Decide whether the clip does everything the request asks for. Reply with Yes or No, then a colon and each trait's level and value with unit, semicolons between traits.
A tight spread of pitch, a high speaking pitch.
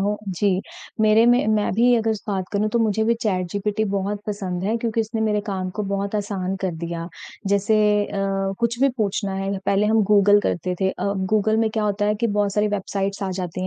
Yes: narrow, 2.0 semitones; high, 205 Hz